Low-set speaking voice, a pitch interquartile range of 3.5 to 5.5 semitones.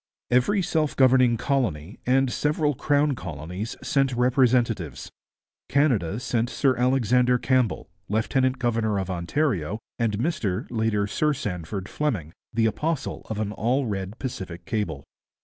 Yes: low, 120 Hz; average, 4.7 semitones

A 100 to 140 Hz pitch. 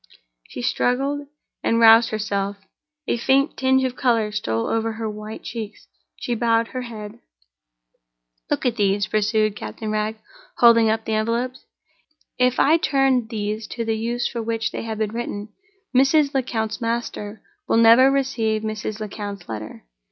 No: high, 225 Hz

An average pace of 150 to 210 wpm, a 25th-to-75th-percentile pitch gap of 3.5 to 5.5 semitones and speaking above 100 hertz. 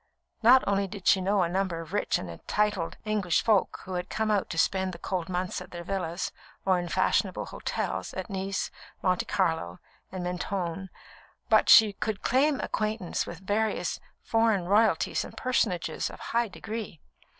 No: average, 170 wpm; average, 3.1 semitones; high, 190 Hz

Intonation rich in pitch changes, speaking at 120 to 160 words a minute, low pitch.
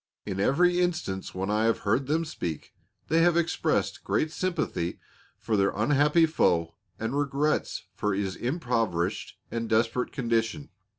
Yes: wide, 7.1 semitones; average, 140 wpm; low, 120 Hz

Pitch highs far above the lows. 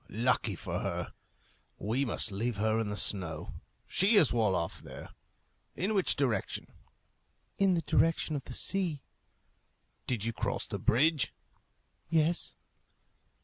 Yes: wide, 7.1 semitones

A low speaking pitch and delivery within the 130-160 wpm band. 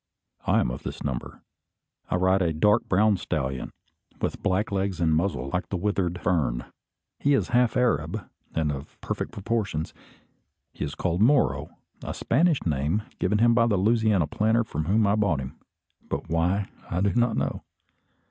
No: very low, 95 Hz; average, 170 wpm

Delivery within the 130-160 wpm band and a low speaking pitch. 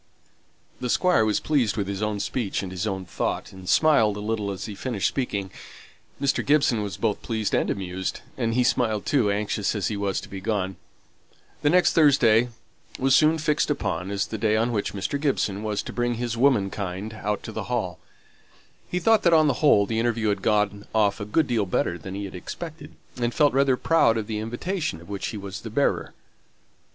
No: fast, 205 wpm; low, 110 Hz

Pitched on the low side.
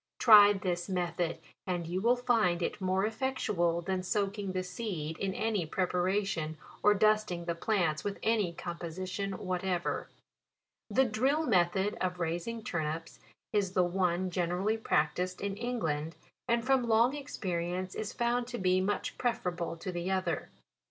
No: medium, 185 Hz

